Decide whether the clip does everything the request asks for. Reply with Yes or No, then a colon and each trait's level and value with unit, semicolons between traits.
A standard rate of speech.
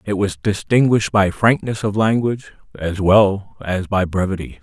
Yes: average, 155 wpm